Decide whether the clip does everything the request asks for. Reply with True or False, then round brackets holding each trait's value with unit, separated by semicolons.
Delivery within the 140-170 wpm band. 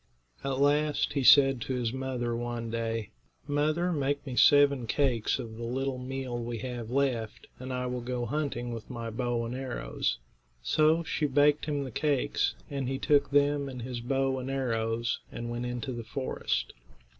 False (180 wpm)